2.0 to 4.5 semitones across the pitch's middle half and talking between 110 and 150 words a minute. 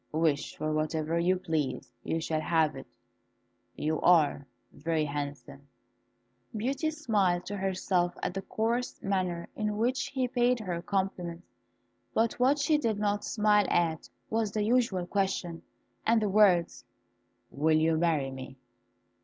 No: average, 5.2 semitones; average, 140 wpm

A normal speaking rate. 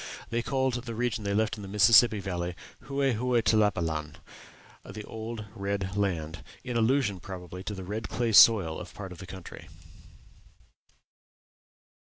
Yes: average, 155 wpm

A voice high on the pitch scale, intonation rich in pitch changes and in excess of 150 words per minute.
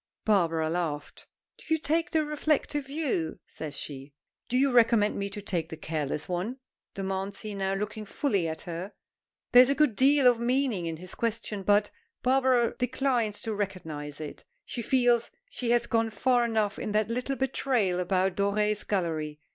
Yes: high, 210 Hz; wide, 5.7 semitones; average, 170 wpm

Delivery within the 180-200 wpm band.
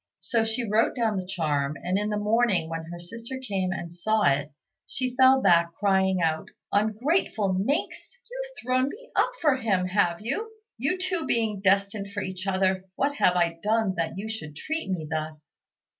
Yes: average, 185 wpm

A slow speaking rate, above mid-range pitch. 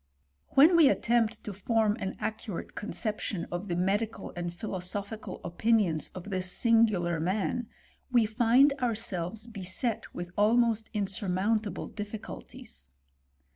Yes: slow, 120 wpm; high, 210 Hz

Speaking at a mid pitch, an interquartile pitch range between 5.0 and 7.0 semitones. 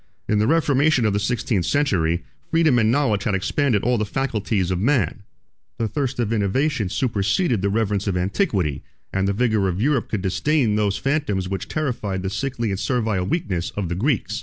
No: low, 110 Hz; wide, 5.5 semitones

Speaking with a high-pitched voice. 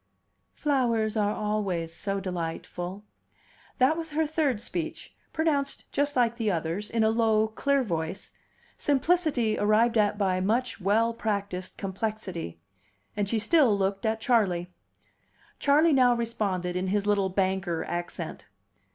Yes: high, 215 Hz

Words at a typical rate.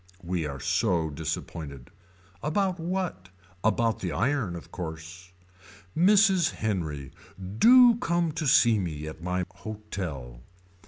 No: slow, 115 wpm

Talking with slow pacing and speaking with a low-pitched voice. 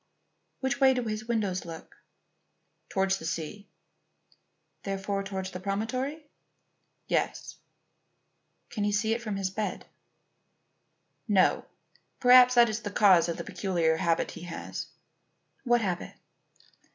No: slow, 125 wpm; high, 205 Hz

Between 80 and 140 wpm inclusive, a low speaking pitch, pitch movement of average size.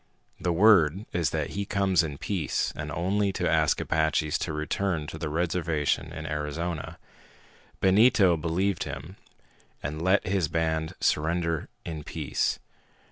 Yes: slow, 135 wpm; very low, 80 Hz; average, 3.4 semitones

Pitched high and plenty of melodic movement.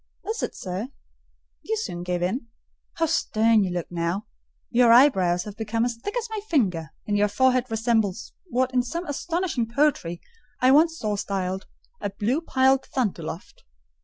Yes: high, 230 Hz; wide, 5.8 semitones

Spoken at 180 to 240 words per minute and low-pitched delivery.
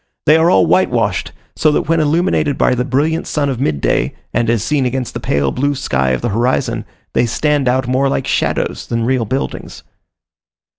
Yes: average, 190 wpm; low, 130 Hz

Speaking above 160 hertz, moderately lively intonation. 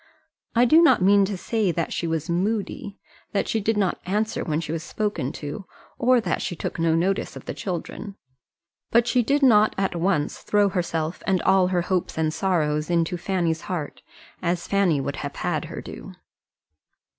Yes: medium, 185 Hz; average, 3.8 semitones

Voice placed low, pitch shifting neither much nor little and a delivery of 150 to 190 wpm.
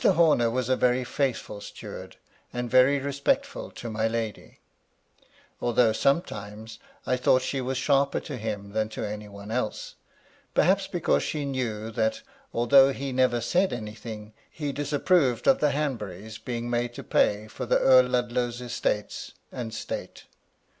Yes: low, 120 Hz; average, 3.8 semitones; average, 155 wpm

